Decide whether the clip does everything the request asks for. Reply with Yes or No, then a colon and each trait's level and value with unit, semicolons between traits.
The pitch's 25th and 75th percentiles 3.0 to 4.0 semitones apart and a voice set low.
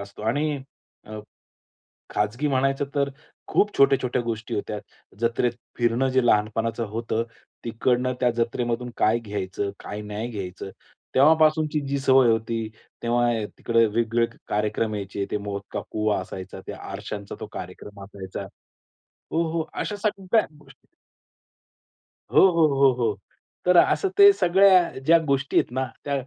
No: average, 4.6 semitones; low, 120 Hz